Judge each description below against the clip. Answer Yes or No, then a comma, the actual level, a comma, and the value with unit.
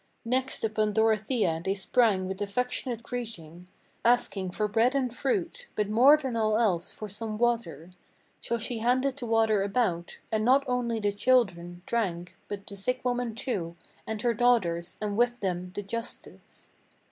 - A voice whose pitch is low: No, high, 220 Hz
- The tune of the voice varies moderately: Yes, average, 3.9 semitones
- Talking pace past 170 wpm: No, average, 165 wpm